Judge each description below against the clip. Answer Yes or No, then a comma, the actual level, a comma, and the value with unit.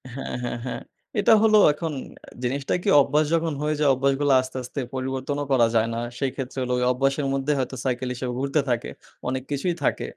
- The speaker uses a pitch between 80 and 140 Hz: Yes, low, 135 Hz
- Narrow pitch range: Yes, narrow, 2.3 semitones